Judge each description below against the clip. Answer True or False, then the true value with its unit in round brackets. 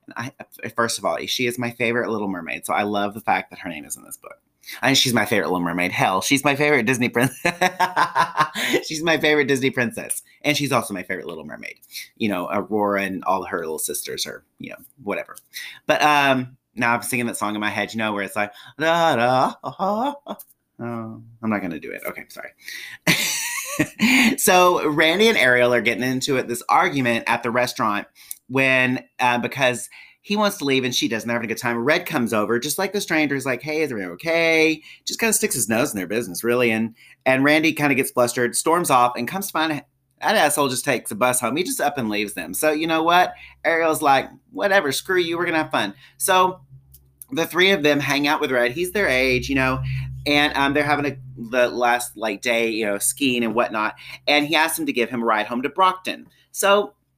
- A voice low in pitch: True (130 Hz)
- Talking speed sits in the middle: False (230 wpm)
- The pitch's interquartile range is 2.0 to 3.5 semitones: False (5.0 semitones)